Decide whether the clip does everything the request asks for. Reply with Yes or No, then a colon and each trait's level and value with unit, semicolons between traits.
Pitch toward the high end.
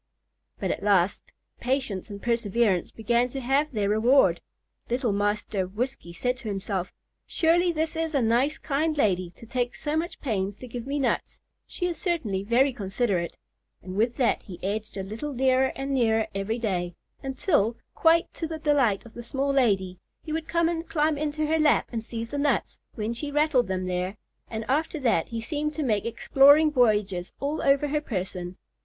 Yes: high, 245 Hz